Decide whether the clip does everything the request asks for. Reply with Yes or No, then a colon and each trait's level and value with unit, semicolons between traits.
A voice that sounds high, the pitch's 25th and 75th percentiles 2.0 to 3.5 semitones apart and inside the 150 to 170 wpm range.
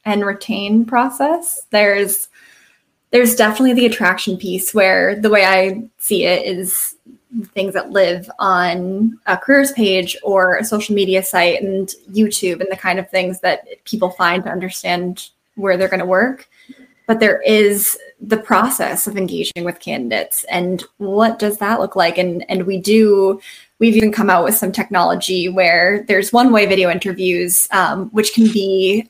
Yes: high, 195 Hz; average, 2.9 semitones; average, 165 wpm